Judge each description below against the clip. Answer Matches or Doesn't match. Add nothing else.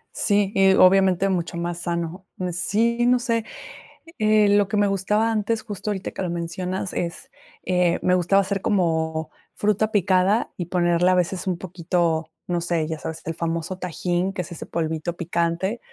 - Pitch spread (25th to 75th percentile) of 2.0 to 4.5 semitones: Matches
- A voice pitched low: Doesn't match